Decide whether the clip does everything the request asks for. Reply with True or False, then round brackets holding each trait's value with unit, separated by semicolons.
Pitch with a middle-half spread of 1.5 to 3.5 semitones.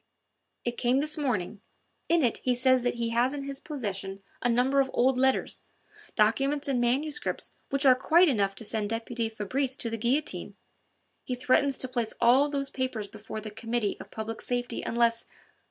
True (3.1 semitones)